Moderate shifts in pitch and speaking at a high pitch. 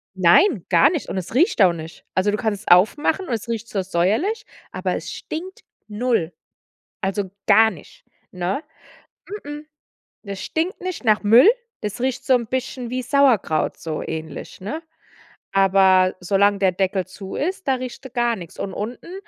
No: wide, 5.8 semitones; high, 215 Hz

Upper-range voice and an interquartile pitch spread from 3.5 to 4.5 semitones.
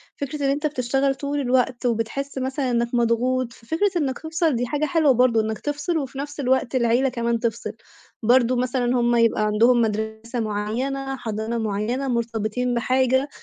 No: very high, 250 Hz; average, 2.8 semitones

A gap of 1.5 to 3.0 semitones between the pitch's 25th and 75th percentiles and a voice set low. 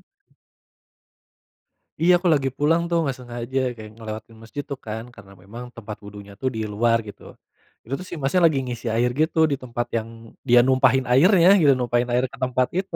No: average, 3.7 semitones; low, 125 Hz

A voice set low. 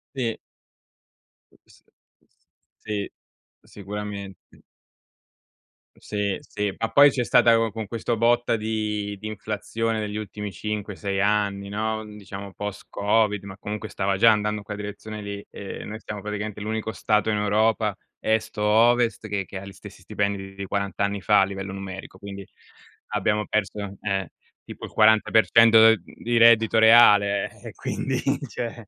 Yes: low, 105 Hz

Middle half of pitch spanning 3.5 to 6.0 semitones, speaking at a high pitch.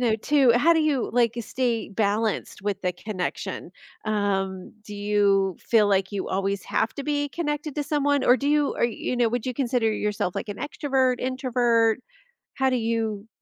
Yes: average, 4.4 semitones; high, 230 Hz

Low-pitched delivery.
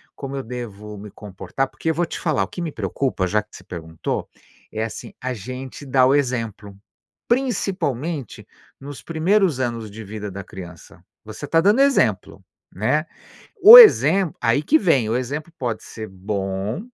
Yes: low, 125 Hz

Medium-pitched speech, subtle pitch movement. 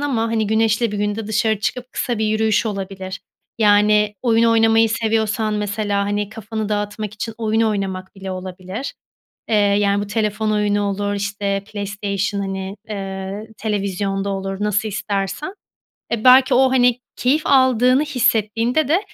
No: high, 210 Hz; narrow, 2.0 semitones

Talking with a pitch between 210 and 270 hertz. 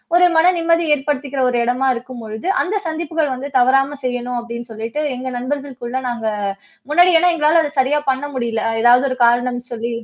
Yes: very high, 260 Hz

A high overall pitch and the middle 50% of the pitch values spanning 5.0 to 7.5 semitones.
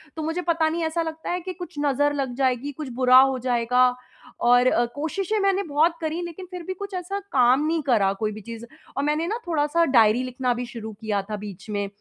Yes: very high, 285 Hz; wide, 5.4 semitones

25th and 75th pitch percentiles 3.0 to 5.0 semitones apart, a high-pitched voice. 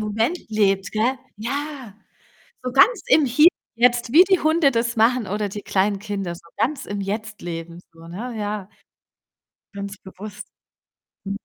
Yes: average, 4.1 semitones; high, 215 Hz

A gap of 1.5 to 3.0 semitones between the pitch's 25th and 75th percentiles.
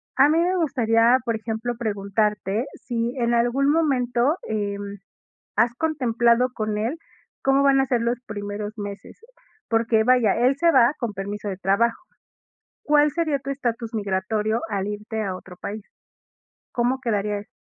No: average, 3.5 semitones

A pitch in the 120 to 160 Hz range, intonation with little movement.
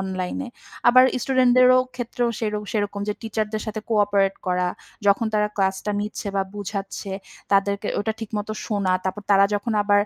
No: high, 205 Hz; narrow, 2.1 semitones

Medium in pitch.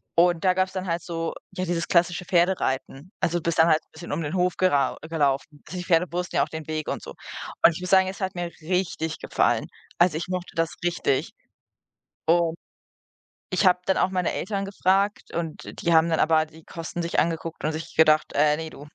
Yes: medium, 170 Hz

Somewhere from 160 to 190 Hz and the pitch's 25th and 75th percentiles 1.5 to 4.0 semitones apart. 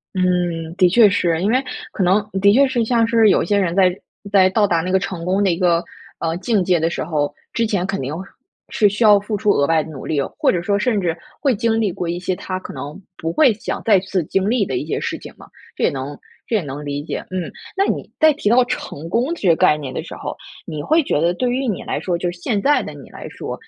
No: medium, 185 Hz; average, 4.5 semitones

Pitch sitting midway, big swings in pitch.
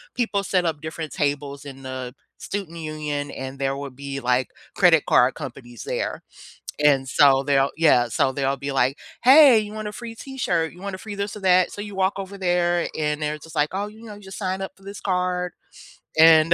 Yes: medium, 160 Hz; wide, 5.8 semitones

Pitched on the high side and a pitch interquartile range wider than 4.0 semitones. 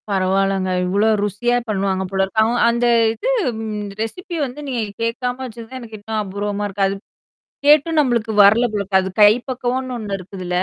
No: high, 215 Hz; average, 3.7 semitones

